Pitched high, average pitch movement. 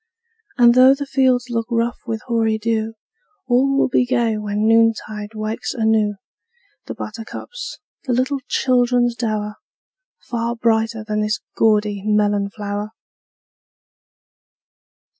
No: high, 225 Hz; narrow, 2.3 semitones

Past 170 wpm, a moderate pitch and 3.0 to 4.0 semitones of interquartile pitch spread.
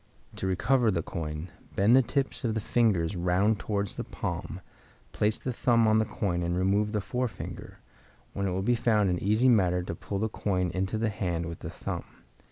No: average, 200 wpm; low, 100 Hz; average, 3.6 semitones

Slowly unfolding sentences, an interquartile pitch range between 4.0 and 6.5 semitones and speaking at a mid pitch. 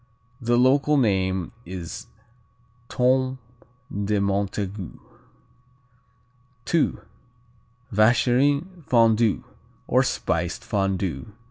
No: slow, 70 wpm; average, 5.0 semitones; low, 110 Hz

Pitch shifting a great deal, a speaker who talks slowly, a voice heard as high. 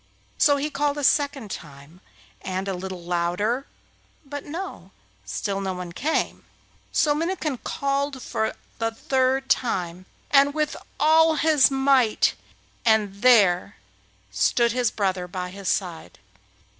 Yes: wide, 7.3 semitones; slow, 130 wpm; high, 235 Hz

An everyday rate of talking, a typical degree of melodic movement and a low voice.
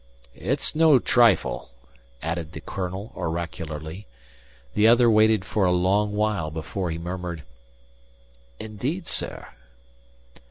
No: slow, 110 wpm; average, 4.6 semitones; very low, 95 Hz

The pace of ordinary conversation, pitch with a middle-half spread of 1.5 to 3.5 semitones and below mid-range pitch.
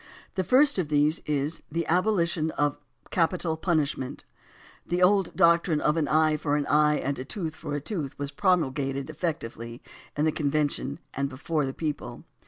No: average, 170 wpm; average, 2.9 semitones; medium, 150 Hz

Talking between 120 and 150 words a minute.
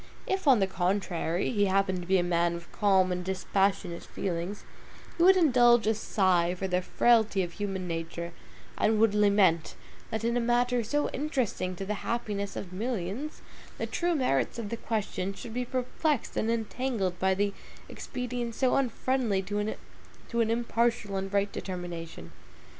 No: average, 160 wpm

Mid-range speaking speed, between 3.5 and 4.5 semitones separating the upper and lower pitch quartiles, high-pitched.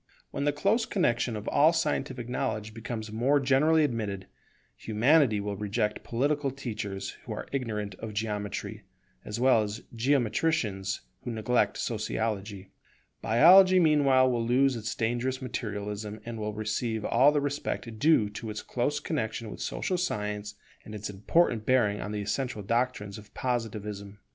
No: average, 150 wpm; average, 4.2 semitones; low, 115 Hz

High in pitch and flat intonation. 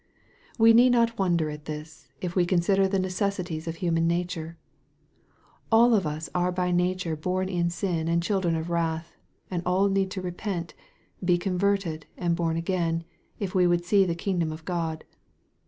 No: medium, 175 Hz; narrow, 2.3 semitones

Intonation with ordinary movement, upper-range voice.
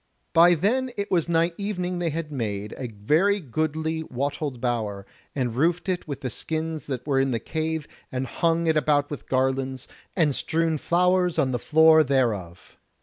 No: average, 4.3 semitones; medium, 155 Hz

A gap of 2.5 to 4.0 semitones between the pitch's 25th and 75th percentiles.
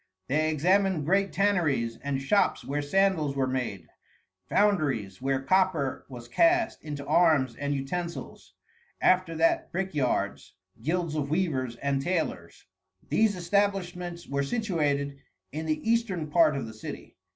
No: average, 5.2 semitones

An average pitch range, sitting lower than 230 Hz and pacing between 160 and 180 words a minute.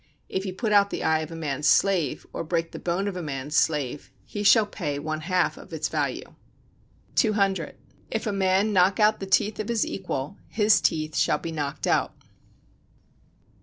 No: average, 4.6 semitones; medium, 185 Hz; average, 190 wpm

